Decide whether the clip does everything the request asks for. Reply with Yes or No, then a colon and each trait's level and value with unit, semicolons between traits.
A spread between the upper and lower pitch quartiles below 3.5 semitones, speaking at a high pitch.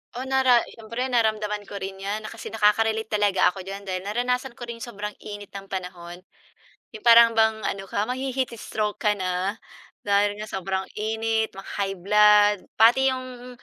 Yes: average, 2.7 semitones; high, 210 Hz